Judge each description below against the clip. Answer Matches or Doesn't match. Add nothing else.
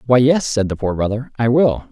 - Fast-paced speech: Matches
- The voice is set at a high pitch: Doesn't match